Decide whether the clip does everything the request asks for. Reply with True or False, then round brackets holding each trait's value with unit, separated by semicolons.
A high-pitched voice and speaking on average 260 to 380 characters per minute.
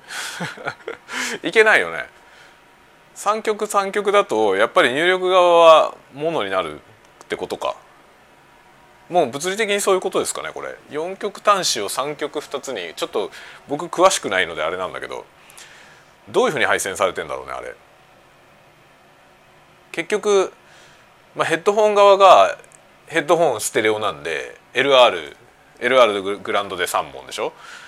True (200 Hz; 280 characters per minute)